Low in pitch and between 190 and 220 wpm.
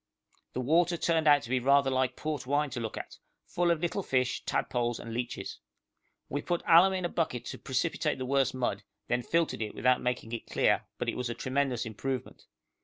Yes: low, 130 Hz; fast, 205 wpm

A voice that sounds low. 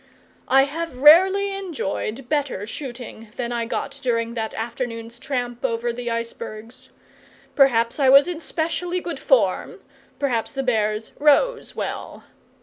No: very high, 255 Hz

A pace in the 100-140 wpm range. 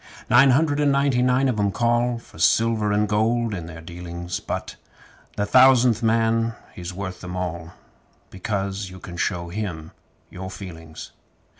No: average, 155 wpm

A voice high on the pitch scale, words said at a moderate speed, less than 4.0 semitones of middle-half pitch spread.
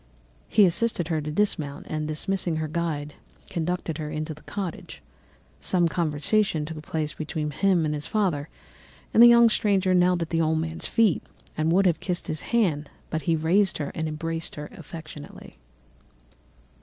No: medium, 165 Hz; average, 170 wpm; average, 3.1 semitones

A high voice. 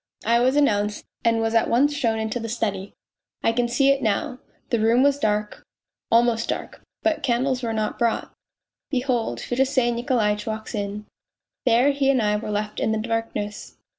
Yes: high, 230 Hz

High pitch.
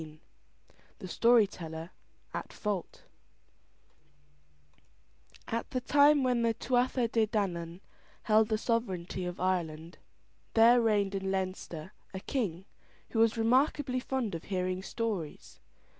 Yes: high, 210 Hz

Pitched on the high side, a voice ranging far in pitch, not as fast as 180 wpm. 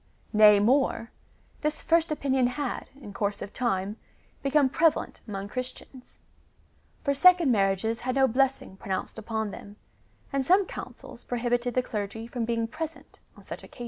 No: high, 245 Hz; average, 4.5 semitones; average, 155 wpm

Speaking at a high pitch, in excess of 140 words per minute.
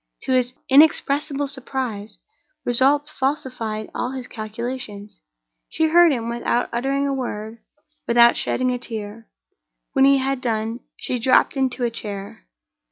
No: very high, 250 Hz; slow, 135 wpm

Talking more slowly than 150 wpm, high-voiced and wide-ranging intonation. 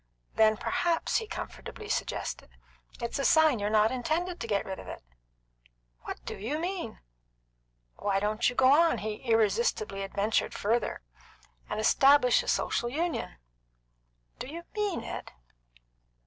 Yes: average, 140 wpm; high, 240 Hz; wide, 7.0 semitones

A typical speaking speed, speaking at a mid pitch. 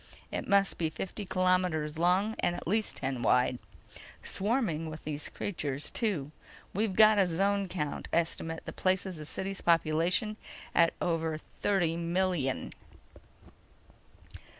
No: slow, 125 wpm; medium, 175 Hz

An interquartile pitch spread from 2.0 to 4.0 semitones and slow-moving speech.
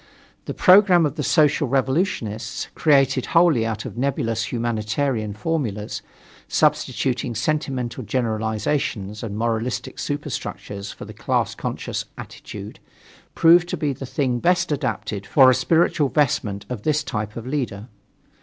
No: average, 5.1 semitones; slow, 130 wpm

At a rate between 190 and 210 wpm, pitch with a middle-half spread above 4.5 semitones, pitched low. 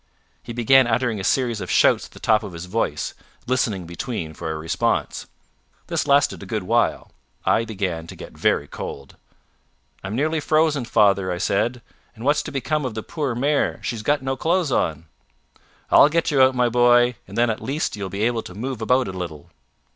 Yes: average, 200 wpm; wide, 5.4 semitones; low, 115 Hz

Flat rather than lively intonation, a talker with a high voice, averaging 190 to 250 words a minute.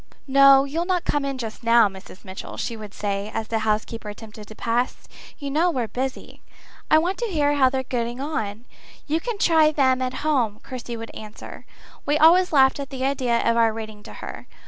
No: average, 4.6 semitones; very high, 255 Hz; fast, 205 wpm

